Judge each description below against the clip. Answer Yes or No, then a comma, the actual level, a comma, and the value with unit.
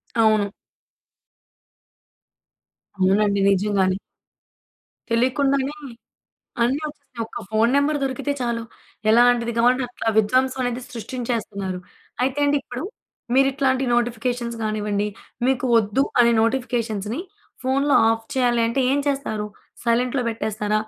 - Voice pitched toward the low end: No, high, 235 Hz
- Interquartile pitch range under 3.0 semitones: No, average, 3.3 semitones